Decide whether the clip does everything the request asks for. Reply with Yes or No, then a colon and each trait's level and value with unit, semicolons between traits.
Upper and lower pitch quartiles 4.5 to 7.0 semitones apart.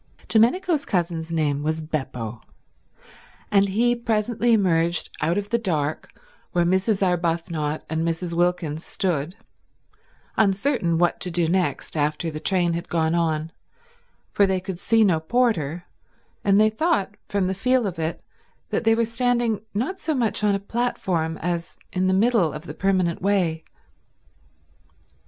Yes: average, 4.8 semitones